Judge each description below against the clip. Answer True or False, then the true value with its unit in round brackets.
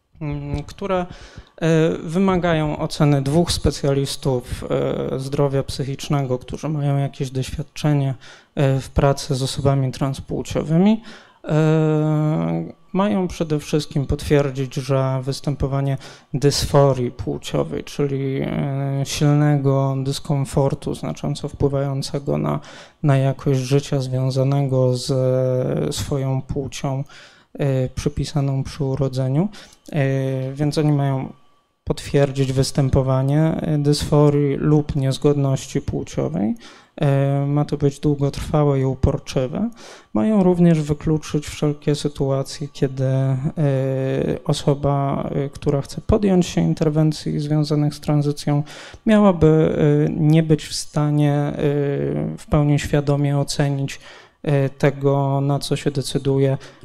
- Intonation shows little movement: True (1.8 semitones)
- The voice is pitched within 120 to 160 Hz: True (140 Hz)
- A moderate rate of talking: False (90 wpm)